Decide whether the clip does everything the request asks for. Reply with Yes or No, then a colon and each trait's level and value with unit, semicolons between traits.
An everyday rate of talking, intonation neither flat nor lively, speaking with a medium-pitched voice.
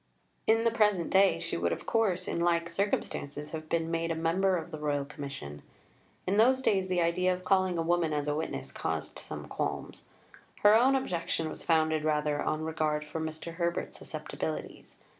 Yes: average, 185 wpm; average, 3.4 semitones; medium, 165 Hz